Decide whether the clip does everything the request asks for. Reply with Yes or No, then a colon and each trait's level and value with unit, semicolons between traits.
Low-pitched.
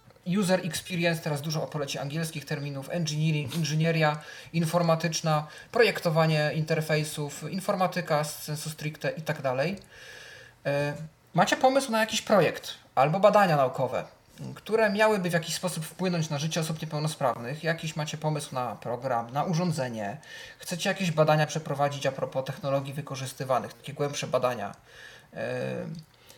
No: medium, 155 Hz